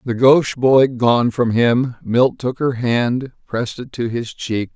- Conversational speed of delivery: Yes, average, 190 wpm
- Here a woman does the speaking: No, male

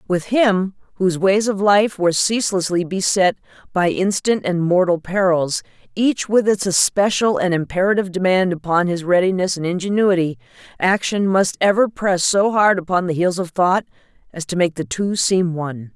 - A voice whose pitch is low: No, medium, 185 Hz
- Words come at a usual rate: Yes, average, 165 wpm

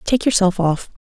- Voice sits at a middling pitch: No, high, 200 Hz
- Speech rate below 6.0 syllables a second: Yes, 4.8 syllables/s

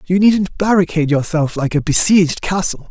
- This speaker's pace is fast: No, average, 165 wpm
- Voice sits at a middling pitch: Yes, medium, 170 Hz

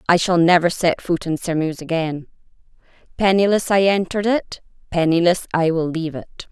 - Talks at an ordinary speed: Yes, average, 155 wpm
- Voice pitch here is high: No, medium, 175 Hz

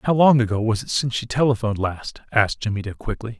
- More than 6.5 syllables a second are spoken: Yes, 6.8 syllables/s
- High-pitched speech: No, low, 115 Hz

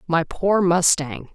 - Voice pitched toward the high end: No, medium, 175 Hz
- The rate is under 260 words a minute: Yes, slow, 135 wpm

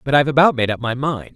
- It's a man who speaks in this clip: Yes, male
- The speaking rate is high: Yes, fast, 310 wpm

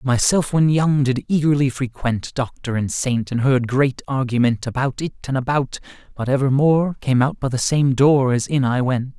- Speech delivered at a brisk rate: No, average, 190 wpm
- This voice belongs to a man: Yes, male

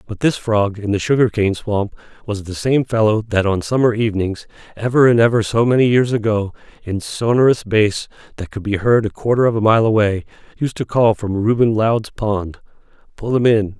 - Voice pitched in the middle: No, low, 110 Hz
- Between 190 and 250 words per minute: Yes, average, 200 wpm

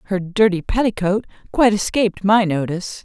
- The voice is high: Yes, high, 200 Hz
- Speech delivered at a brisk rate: No, average, 140 wpm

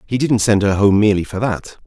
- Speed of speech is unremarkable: No, fast, 260 wpm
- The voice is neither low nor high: No, low, 105 Hz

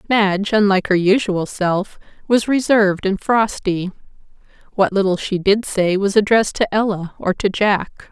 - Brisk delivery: No, average, 155 wpm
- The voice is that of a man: No, female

